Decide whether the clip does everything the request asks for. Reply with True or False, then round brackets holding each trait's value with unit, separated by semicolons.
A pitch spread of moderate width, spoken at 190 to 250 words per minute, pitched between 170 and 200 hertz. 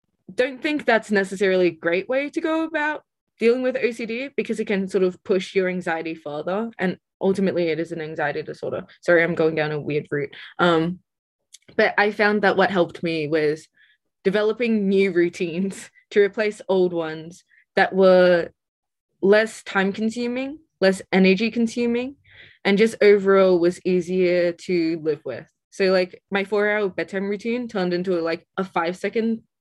False (4.1 semitones; 165 wpm; 190 Hz)